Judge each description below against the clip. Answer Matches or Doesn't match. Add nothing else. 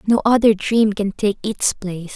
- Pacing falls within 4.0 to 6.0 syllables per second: Matches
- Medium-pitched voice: Doesn't match